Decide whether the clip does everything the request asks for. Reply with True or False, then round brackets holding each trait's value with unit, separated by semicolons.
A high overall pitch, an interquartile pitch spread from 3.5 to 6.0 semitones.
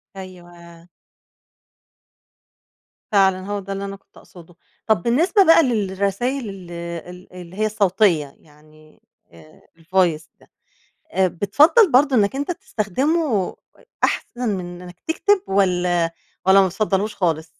True (195 Hz; 4.2 semitones)